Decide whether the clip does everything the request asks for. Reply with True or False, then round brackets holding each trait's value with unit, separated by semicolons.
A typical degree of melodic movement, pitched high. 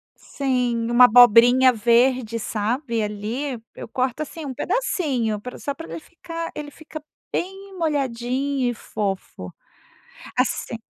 True (4.0 semitones; 255 Hz)